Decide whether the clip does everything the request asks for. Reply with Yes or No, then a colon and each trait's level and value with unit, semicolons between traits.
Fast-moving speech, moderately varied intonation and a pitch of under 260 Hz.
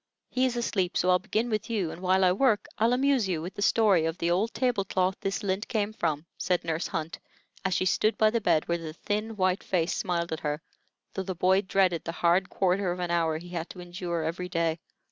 Yes: fast, 240 wpm; average, 3.3 semitones; medium, 185 Hz